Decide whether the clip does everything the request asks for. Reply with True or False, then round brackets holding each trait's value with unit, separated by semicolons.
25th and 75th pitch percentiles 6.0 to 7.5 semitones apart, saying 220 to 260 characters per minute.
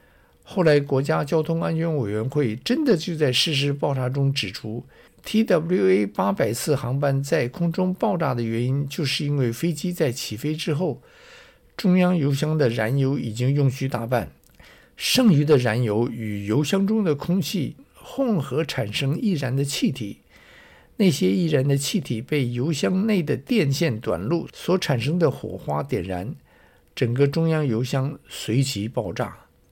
False (5.4 semitones; 235 characters per minute)